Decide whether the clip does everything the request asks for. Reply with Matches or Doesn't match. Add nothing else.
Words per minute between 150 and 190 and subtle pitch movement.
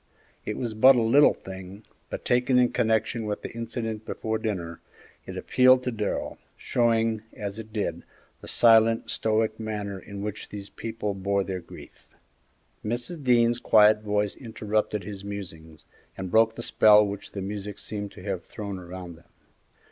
Matches